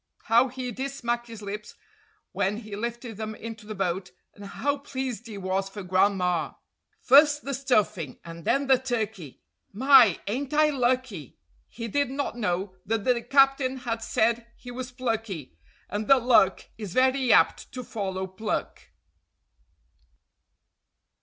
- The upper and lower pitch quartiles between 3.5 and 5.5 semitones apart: Yes, average, 4.4 semitones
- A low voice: No, high, 230 Hz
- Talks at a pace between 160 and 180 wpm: No, average, 145 wpm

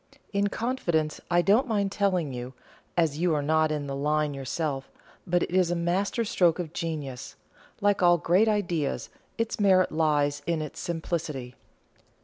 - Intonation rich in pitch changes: No, average, 3.9 semitones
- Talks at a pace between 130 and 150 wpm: No, average, 160 wpm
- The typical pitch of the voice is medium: Yes, medium, 170 Hz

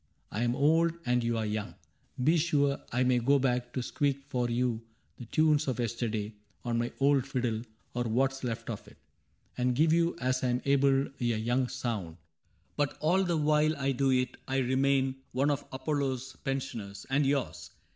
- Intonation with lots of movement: No, narrow, 2.6 semitones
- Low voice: Yes, low, 130 Hz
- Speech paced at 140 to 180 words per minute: No, average, 195 wpm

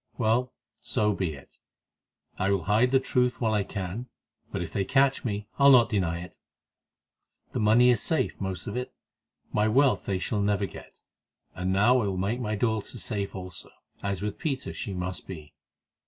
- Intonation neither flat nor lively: Yes, average, 4.4 semitones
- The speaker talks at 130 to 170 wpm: No, average, 185 wpm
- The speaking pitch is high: No, low, 105 Hz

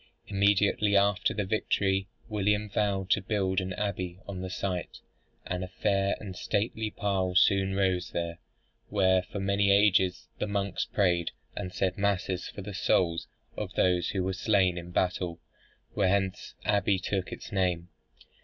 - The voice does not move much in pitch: Yes, narrow, 1.7 semitones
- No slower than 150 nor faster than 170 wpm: Yes, average, 160 wpm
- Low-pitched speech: Yes, very low, 95 Hz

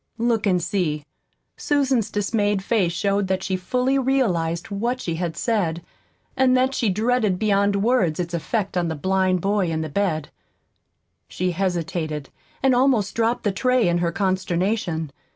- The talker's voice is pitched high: Yes, high, 195 Hz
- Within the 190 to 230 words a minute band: No, average, 155 wpm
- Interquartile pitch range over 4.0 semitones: Yes, average, 4.8 semitones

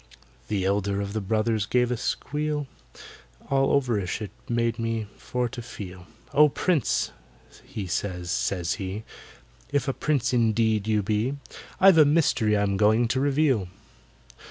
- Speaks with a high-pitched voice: No, low, 115 Hz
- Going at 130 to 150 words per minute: Yes, average, 145 wpm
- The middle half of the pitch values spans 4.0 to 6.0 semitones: Yes, average, 4.6 semitones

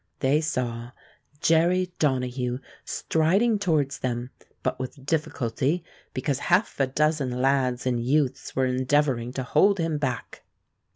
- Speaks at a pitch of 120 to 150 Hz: Yes, low, 135 Hz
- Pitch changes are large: No, average, 3.9 semitones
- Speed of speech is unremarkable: No, slow, 125 wpm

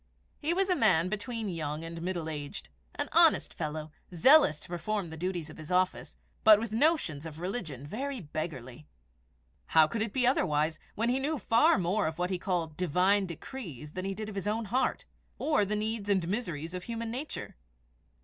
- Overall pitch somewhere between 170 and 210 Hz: Yes, medium, 185 Hz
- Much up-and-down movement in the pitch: Yes, wide, 6.0 semitones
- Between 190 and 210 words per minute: Yes, average, 195 wpm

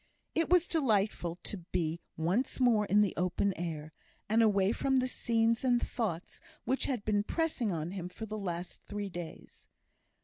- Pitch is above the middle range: Yes, high, 205 Hz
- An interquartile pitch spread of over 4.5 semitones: Yes, average, 5.2 semitones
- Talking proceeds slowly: No, average, 170 wpm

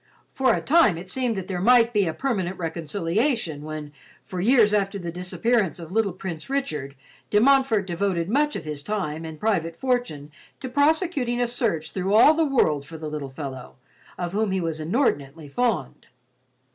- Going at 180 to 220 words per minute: Yes, average, 185 wpm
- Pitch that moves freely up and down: Yes, wide, 7.1 semitones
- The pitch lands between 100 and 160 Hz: No, high, 190 Hz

